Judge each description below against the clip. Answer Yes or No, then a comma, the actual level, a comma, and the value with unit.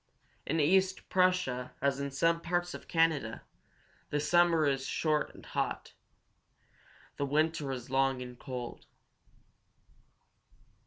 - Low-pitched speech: No, medium, 150 Hz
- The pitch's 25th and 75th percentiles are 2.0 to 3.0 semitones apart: No, average, 3.8 semitones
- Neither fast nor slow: No, slow, 110 wpm